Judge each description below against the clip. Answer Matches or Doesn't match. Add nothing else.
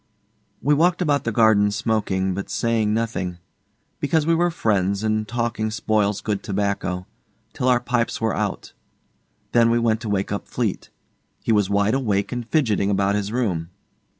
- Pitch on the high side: Doesn't match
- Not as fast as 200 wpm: Matches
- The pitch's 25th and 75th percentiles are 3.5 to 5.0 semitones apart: Doesn't match